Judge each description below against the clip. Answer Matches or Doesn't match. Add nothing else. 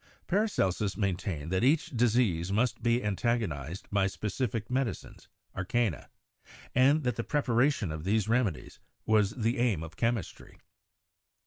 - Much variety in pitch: Doesn't match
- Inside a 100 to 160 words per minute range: Matches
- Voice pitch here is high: Doesn't match